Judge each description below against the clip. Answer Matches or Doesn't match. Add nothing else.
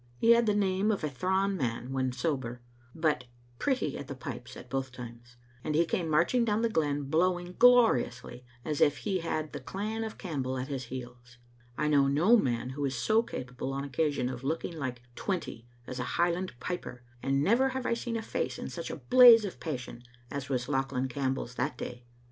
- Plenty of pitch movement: Matches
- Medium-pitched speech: Matches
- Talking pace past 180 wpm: Matches